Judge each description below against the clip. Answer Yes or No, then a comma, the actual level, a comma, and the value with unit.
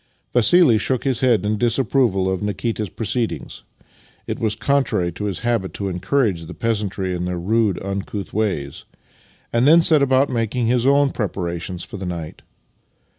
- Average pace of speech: Yes, average, 160 wpm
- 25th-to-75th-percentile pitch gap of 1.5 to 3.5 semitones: No, average, 4.7 semitones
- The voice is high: No, low, 110 Hz